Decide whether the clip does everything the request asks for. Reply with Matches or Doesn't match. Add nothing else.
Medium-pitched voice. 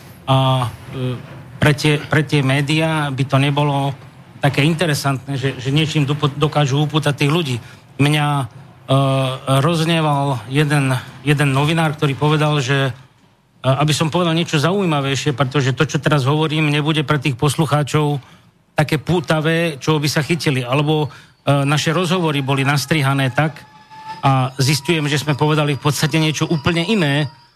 Matches